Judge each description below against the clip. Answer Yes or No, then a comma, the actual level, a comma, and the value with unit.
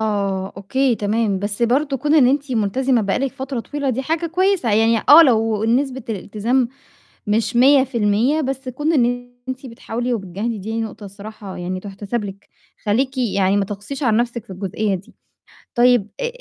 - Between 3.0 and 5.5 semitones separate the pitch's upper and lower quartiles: Yes, average, 4.4 semitones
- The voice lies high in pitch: Yes, high, 230 Hz